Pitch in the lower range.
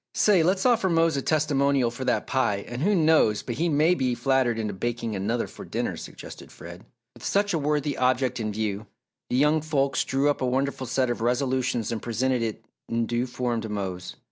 Yes: low, 130 Hz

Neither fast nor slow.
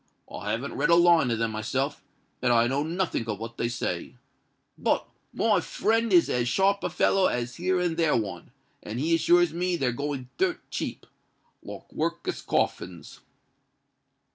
Yes: average, 160 wpm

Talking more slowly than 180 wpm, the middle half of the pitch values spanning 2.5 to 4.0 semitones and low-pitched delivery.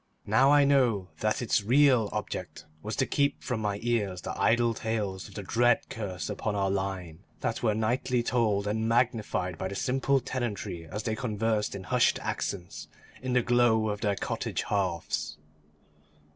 Yes: average, 170 wpm; average, 3.5 semitones; low, 110 Hz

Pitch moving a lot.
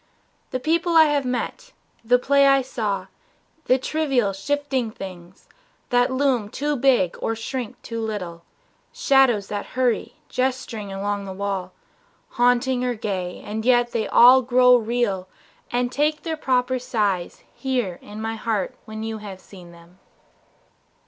No: average, 4.3 semitones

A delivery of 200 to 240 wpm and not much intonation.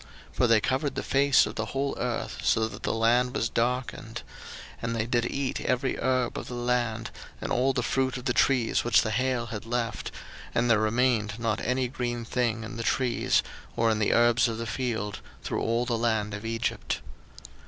Yes: fast, 205 wpm; narrow, 1.8 semitones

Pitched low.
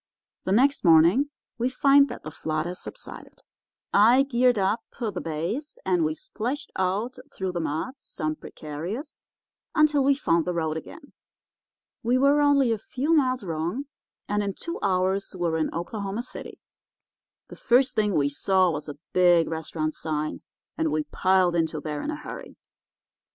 No: high, 190 Hz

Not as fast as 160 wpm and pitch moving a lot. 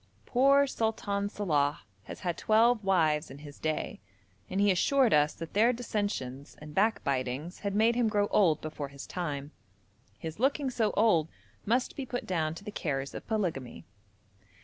No: average, 165 wpm; wide, 6.6 semitones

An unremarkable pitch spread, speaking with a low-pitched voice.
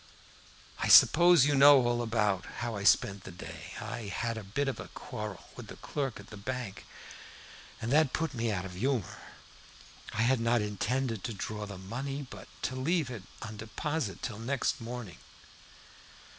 Yes: average, 4.3 semitones; low, 115 Hz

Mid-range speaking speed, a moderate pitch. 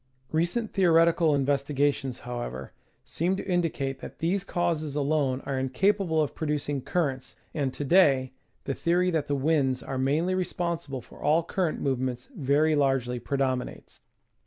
Yes: average, 160 wpm; medium, 145 Hz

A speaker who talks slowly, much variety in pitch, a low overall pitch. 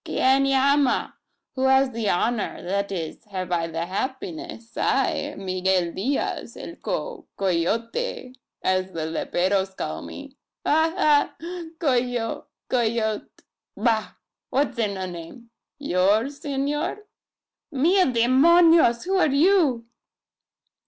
No: slow, 110 wpm; wide, 6.8 semitones; high, 240 Hz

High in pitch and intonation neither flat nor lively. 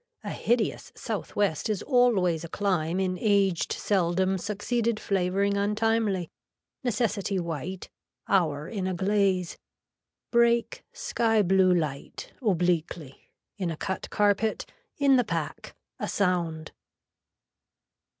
Yes: high, 195 Hz; average, 3.3 semitones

